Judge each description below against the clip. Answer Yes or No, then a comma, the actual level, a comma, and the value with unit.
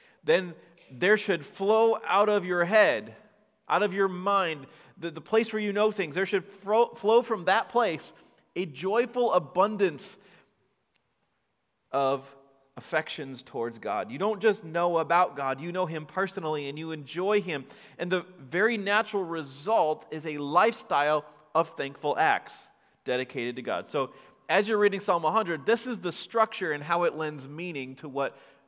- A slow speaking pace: No, average, 165 wpm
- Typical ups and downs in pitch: No, wide, 5.8 semitones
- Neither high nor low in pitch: Yes, medium, 175 Hz